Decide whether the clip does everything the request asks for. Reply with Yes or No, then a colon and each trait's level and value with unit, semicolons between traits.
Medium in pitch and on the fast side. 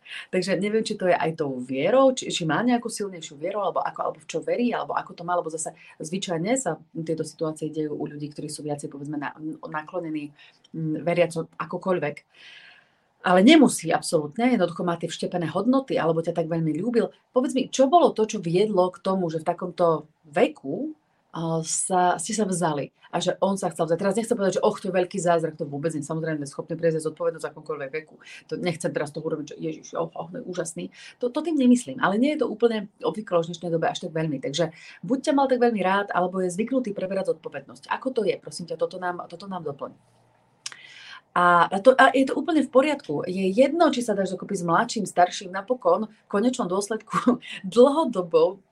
Yes: medium, 180 Hz; fast, 210 wpm